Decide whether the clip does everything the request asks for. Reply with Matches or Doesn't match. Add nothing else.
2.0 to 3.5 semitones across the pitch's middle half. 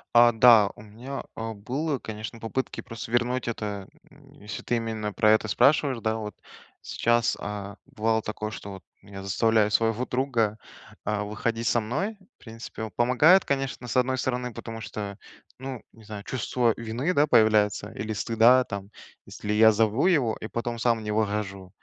Matches